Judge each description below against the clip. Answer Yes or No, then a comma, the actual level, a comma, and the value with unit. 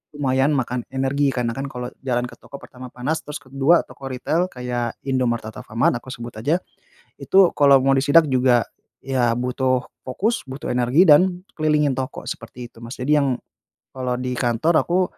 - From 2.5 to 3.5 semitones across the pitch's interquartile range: Yes, average, 2.8 semitones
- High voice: No, low, 130 Hz